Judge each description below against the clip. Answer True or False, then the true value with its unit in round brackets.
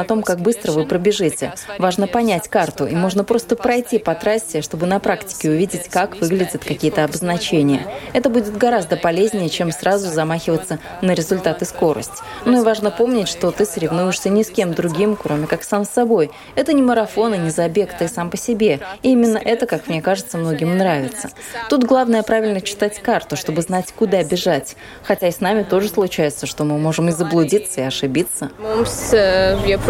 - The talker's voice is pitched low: False (190 Hz)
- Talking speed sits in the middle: False (180 wpm)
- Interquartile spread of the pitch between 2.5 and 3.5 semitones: False (4.4 semitones)